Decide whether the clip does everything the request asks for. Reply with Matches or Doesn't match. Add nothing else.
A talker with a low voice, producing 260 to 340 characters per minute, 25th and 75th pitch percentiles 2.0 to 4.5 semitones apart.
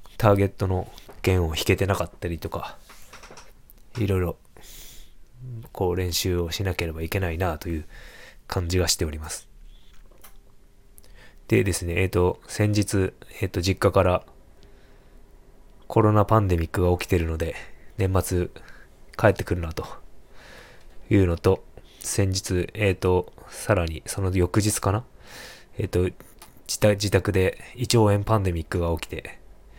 Matches